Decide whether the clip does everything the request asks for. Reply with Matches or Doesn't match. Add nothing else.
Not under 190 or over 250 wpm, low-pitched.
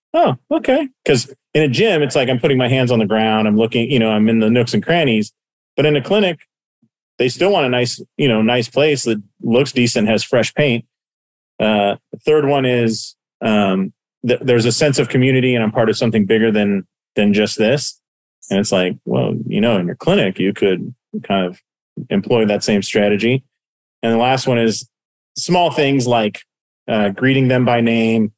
Matches